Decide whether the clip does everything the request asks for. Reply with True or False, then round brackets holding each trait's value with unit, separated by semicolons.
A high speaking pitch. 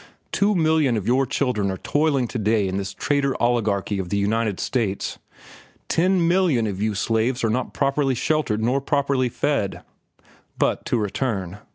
False (120 Hz)